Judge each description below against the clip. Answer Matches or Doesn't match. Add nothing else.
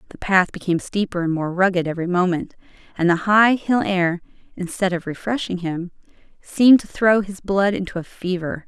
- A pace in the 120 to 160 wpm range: Doesn't match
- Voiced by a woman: Matches